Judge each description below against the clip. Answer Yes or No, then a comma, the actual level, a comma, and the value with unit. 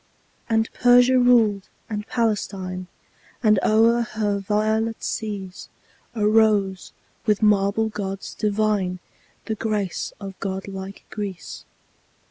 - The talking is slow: Yes, slow, 100 wpm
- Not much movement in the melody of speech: Yes, narrow, 2.1 semitones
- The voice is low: No, high, 210 Hz